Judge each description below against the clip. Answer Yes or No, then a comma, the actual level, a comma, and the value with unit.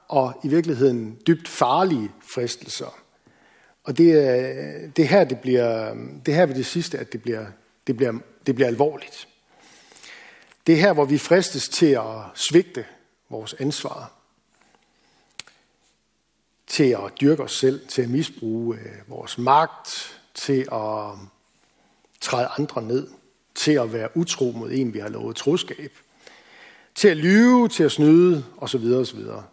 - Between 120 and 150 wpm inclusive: Yes, slow, 145 wpm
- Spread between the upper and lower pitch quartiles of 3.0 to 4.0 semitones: No, average, 5.3 semitones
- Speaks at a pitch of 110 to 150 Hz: Yes, low, 135 Hz